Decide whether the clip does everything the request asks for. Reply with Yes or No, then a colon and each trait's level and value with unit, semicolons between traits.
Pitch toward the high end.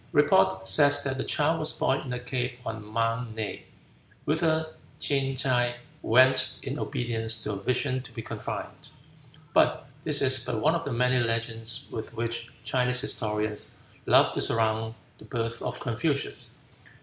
No: low, 125 Hz